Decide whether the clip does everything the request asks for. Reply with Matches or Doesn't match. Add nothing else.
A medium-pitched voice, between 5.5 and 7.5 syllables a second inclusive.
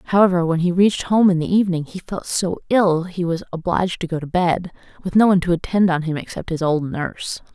Matches